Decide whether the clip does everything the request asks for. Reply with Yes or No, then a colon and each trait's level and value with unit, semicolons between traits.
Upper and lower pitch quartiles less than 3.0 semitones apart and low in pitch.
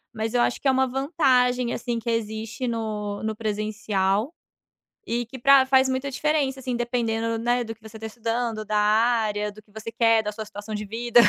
No: narrow, 2.5 semitones; high, 230 Hz